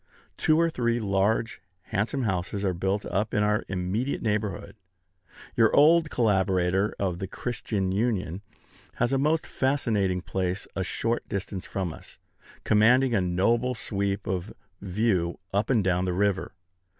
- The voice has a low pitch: Yes, low, 100 Hz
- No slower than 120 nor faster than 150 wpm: Yes, average, 145 wpm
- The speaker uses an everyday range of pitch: Yes, average, 3.7 semitones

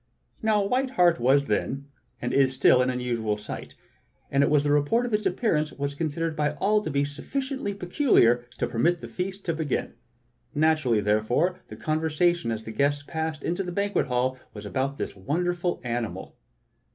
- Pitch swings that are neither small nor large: No, wide, 5.7 semitones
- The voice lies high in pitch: No, medium, 150 Hz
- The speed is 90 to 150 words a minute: No, average, 175 wpm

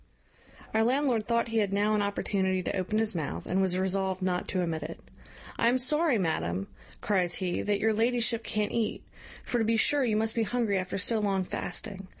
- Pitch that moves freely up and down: No, average, 3.4 semitones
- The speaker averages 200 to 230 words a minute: Yes, fast, 205 wpm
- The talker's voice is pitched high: Yes, high, 210 Hz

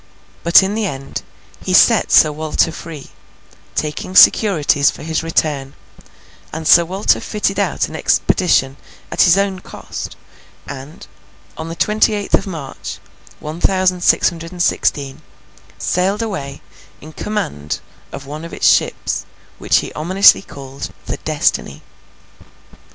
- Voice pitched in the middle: Yes, medium, 165 Hz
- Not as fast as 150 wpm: Yes, average, 140 wpm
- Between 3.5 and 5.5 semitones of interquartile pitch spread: Yes, average, 4.6 semitones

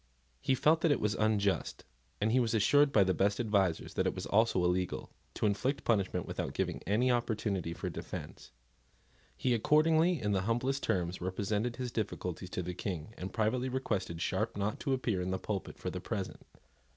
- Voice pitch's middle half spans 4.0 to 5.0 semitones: Yes, average, 4.7 semitones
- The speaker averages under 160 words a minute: No, average, 190 wpm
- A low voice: Yes, low, 105 Hz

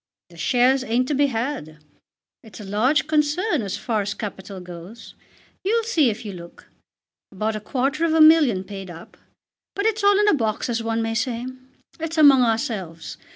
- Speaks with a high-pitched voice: Yes, high, 235 Hz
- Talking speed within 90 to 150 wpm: No, average, 185 wpm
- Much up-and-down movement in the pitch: Yes, wide, 6.6 semitones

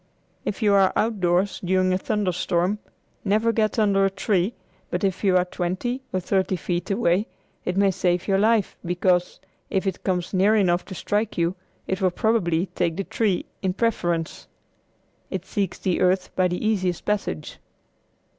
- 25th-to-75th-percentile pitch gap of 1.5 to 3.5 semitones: Yes, narrow, 2.4 semitones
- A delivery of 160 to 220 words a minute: Yes, average, 170 wpm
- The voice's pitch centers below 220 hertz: Yes, high, 190 Hz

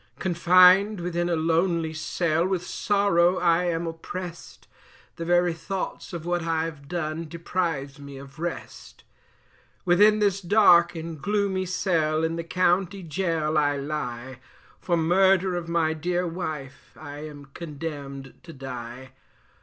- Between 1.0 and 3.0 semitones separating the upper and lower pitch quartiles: Yes, average, 2.7 semitones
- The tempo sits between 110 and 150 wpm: Yes, slow, 135 wpm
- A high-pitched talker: No, medium, 170 Hz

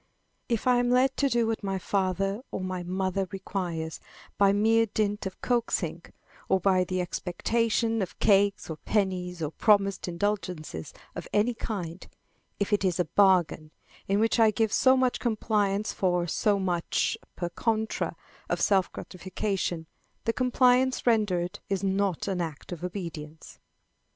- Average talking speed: Yes, average, 150 wpm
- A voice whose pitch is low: No, high, 195 Hz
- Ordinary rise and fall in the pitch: Yes, average, 3.5 semitones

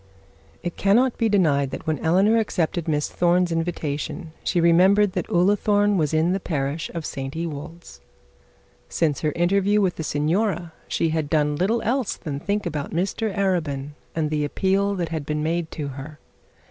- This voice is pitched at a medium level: Yes, medium, 170 Hz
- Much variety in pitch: No, average, 4.3 semitones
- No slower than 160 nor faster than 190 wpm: Yes, average, 170 wpm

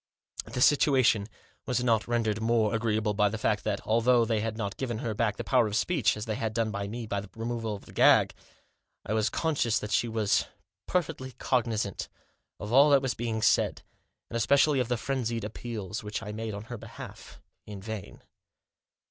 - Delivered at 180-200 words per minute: Yes, average, 190 wpm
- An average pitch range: No, narrow, 2.3 semitones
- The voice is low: Yes, low, 115 Hz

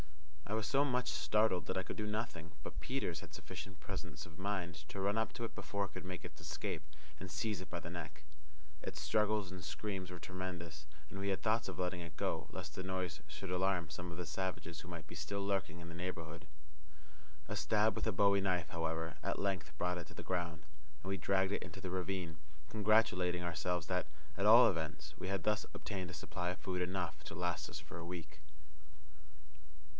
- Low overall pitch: Yes, very low, 90 Hz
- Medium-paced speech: No, fast, 215 wpm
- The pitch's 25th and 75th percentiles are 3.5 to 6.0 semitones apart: No, average, 2.8 semitones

